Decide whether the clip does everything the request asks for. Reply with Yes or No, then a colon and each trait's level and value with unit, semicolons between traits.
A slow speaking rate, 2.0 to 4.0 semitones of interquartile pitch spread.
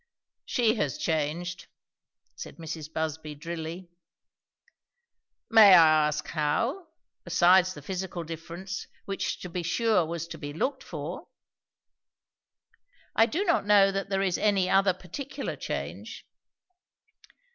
Yes: slow, 120 wpm; average, 3.6 semitones